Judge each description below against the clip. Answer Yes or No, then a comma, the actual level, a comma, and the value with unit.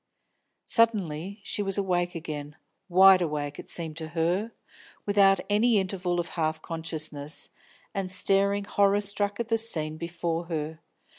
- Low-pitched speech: No, medium, 180 Hz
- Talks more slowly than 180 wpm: Yes, average, 140 wpm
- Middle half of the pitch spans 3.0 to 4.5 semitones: Yes, average, 3.9 semitones